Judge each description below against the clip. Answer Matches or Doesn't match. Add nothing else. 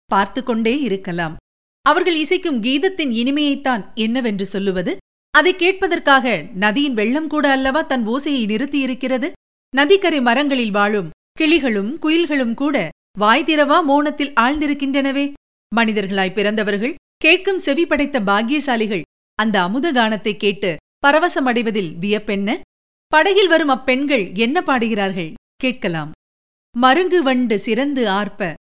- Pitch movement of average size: Doesn't match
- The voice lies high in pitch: Matches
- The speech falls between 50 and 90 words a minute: Doesn't match